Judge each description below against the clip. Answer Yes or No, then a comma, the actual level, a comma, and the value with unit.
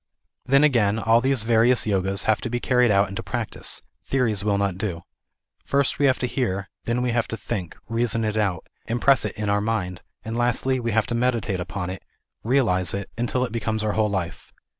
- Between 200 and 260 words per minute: Yes, fast, 205 wpm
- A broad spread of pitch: No, average, 3.4 semitones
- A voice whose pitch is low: Yes, low, 110 Hz